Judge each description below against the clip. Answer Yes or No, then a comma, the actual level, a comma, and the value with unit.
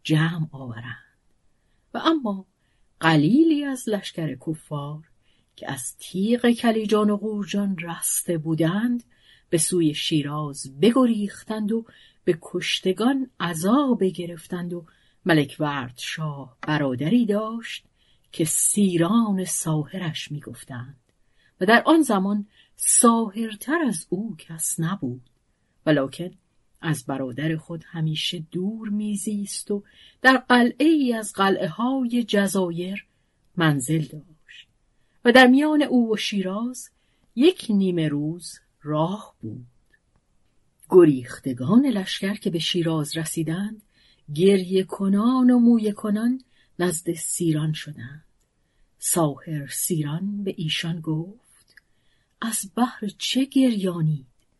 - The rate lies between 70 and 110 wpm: Yes, slow, 105 wpm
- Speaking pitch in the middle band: Yes, medium, 180 Hz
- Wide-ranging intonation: Yes, wide, 5.8 semitones